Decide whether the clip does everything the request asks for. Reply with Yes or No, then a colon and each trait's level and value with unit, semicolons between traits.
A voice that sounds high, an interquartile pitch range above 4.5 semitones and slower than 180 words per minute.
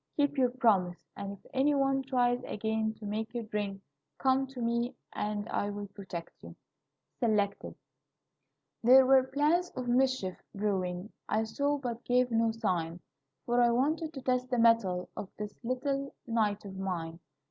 No: high, 230 Hz; average, 4.2 semitones; average, 160 wpm